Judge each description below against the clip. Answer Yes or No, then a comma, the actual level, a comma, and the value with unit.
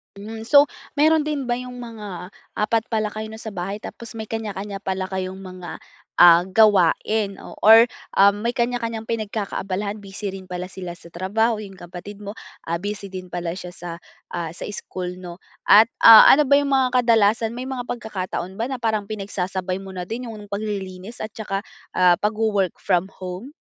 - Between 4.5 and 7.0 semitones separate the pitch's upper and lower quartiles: No, average, 3.3 semitones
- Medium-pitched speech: No, high, 205 Hz